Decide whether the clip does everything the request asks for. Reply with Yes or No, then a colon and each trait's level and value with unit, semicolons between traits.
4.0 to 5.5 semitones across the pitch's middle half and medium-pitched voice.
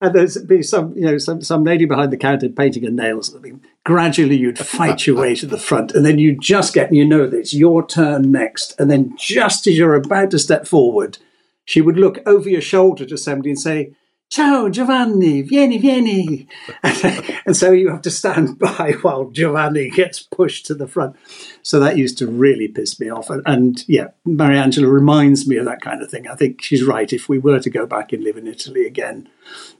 Yes: average, 5.1 semitones; medium, 155 Hz